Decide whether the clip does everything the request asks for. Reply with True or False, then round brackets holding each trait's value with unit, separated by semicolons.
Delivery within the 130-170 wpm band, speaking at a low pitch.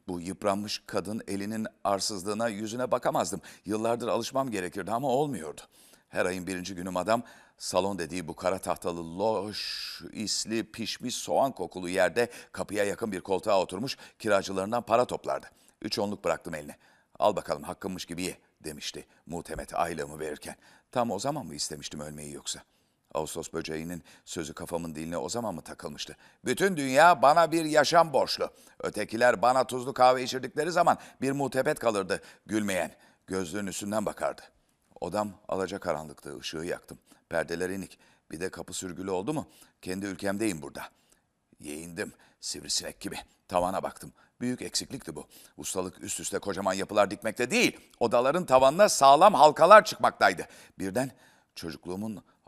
True (140 wpm; 100 Hz)